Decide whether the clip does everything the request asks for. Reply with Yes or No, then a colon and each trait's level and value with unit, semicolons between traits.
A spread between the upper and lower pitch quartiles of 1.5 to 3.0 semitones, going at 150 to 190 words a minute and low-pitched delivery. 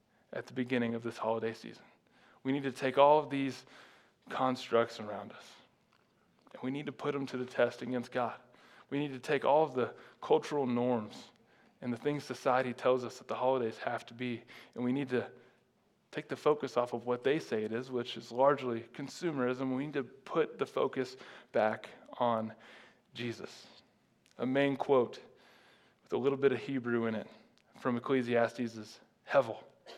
Yes: narrow, 2.5 semitones; average, 180 wpm; low, 125 Hz